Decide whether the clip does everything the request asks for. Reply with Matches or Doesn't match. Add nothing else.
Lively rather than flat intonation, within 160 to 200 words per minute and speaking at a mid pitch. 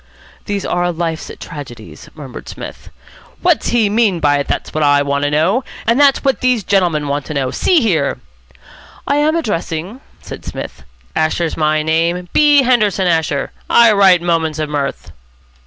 Matches